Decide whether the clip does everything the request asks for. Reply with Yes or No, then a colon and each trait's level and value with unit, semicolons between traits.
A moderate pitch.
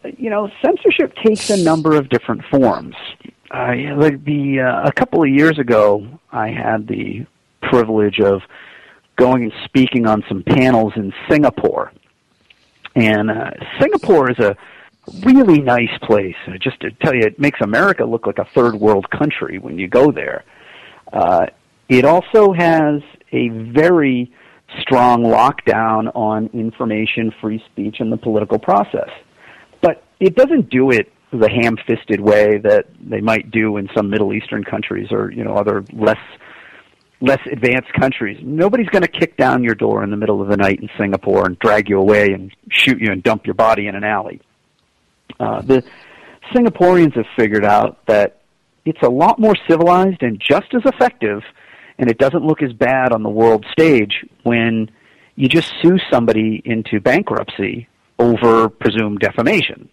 No: low, 120 Hz